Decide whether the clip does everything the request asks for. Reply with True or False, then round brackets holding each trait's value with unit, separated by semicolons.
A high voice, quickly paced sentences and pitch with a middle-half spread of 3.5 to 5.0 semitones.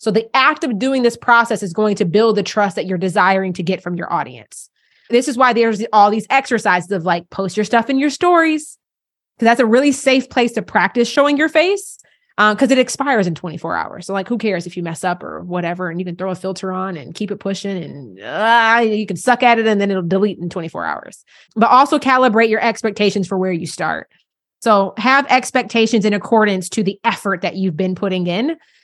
True (215 Hz; 230 wpm; 4.5 semitones)